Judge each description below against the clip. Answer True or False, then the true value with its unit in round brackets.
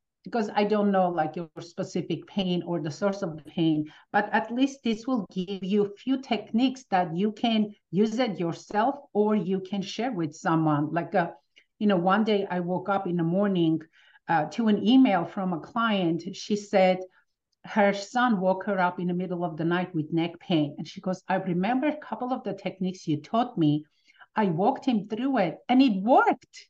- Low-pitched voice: False (190 Hz)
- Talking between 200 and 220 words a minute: True (205 wpm)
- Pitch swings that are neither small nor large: True (3.6 semitones)